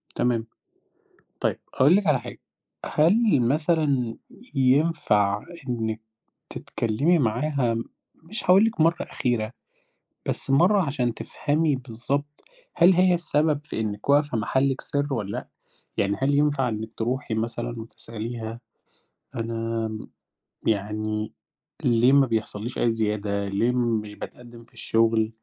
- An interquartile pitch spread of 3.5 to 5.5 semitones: Yes, average, 4.6 semitones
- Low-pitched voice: Yes, low, 120 Hz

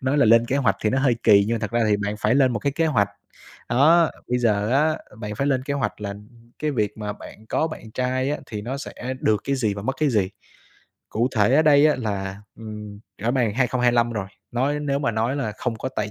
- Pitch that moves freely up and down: No, average, 4.4 semitones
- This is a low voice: Yes, low, 120 Hz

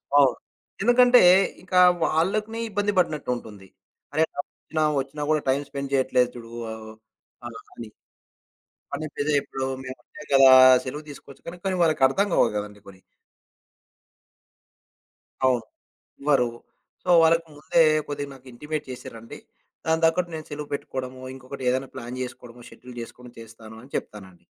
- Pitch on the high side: No, low, 135 Hz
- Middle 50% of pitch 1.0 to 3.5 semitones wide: No, average, 4.2 semitones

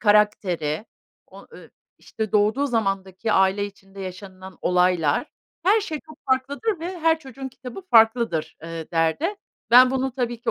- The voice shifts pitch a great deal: Yes, wide, 6.0 semitones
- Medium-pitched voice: No, high, 220 Hz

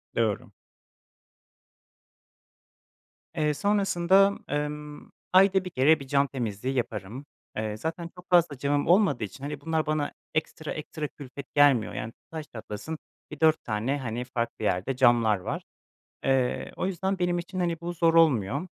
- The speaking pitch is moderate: Yes, medium, 145 Hz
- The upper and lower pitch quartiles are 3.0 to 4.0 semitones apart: No, wide, 5.4 semitones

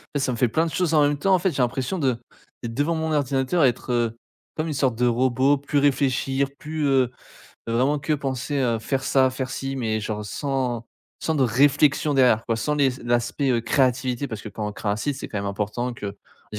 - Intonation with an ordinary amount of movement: Yes, average, 3.3 semitones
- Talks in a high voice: No, low, 130 Hz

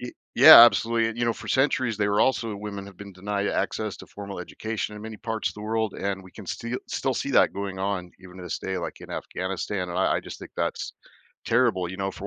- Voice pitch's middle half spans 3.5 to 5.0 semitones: No, average, 2.9 semitones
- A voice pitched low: Yes, low, 105 Hz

